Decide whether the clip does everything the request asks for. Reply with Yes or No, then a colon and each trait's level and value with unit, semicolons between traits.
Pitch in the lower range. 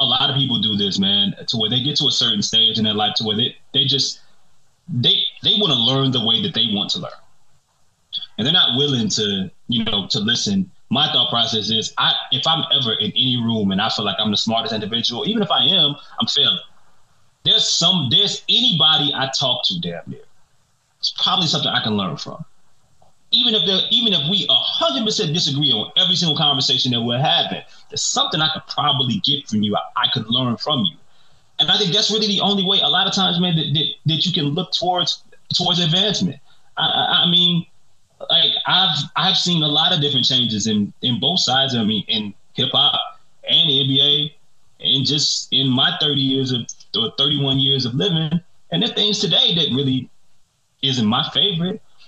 No: medium, 145 Hz